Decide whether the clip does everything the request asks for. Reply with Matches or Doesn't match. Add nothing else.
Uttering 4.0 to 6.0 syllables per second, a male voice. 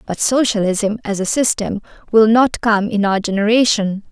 Doesn't match